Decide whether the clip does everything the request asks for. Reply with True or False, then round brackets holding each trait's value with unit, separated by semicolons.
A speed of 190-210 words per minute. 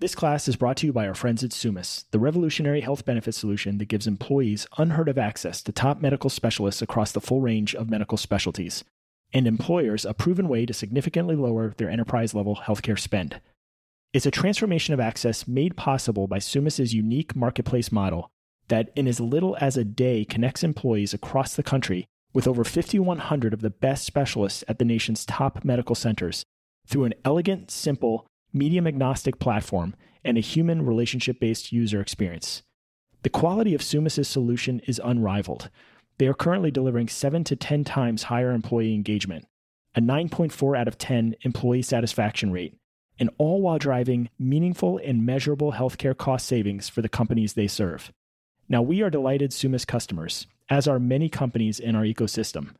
False (170 wpm)